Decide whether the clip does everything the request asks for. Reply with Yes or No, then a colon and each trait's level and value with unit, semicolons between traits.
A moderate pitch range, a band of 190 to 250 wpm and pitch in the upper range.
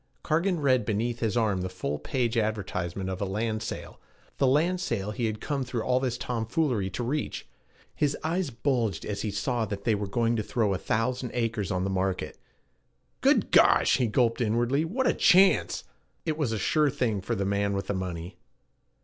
No: average, 4.3 semitones; average, 195 wpm; low, 115 Hz